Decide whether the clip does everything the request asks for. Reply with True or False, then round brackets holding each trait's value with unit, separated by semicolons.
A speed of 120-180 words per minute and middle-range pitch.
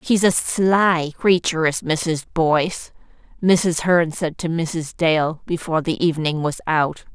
True (150 wpm; 165 Hz)